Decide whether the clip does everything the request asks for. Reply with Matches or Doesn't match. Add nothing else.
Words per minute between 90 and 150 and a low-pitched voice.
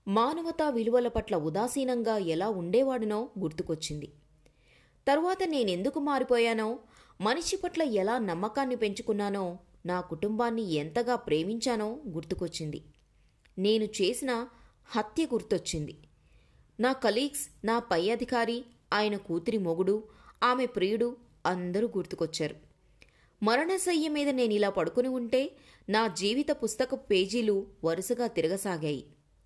Doesn't match